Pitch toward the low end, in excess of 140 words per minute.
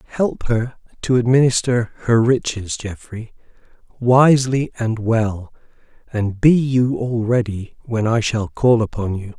No: low, 115 Hz; slow, 135 wpm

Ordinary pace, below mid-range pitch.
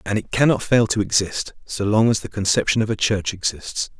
No: fast, 225 wpm; low, 105 Hz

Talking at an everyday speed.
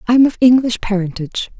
Yes: average, 190 wpm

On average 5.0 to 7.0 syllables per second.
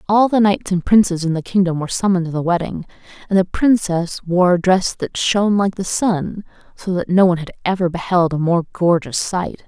Yes: 5.5 syllables/s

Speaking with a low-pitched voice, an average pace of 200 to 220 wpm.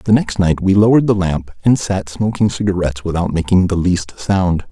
Yes: very low, 95 Hz; fast, 205 wpm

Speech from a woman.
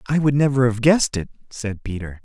No: male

